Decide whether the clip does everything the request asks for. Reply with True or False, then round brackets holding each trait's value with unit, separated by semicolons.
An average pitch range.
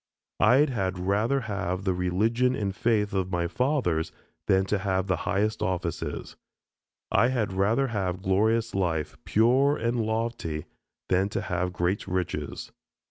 True (3.9 semitones)